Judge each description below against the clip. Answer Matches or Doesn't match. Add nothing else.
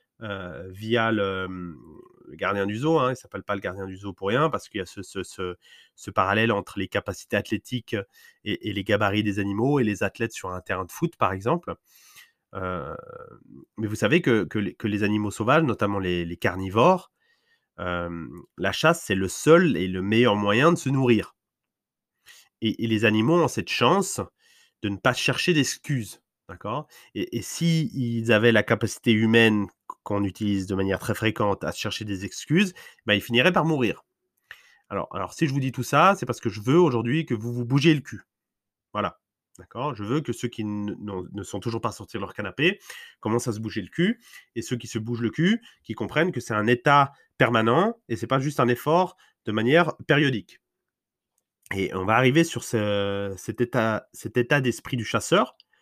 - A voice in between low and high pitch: Doesn't match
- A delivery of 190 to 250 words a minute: Matches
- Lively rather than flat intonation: Matches